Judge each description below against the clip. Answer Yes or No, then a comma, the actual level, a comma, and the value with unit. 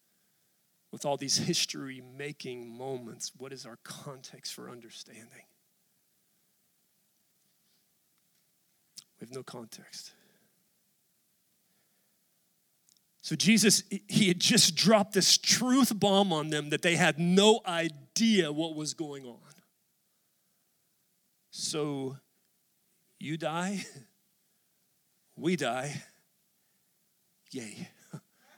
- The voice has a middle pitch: Yes, medium, 180 Hz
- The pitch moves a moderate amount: Yes, average, 5.0 semitones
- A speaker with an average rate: No, slow, 90 wpm